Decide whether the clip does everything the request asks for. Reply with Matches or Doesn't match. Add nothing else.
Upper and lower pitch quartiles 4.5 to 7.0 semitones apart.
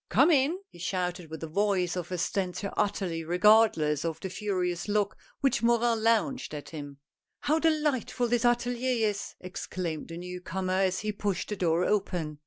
Matches